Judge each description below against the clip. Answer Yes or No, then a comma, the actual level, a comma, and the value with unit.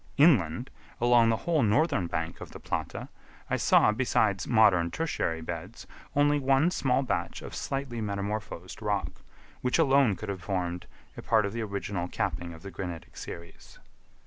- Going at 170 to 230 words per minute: No, average, 160 wpm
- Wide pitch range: Yes, wide, 6.5 semitones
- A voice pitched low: Yes, low, 105 Hz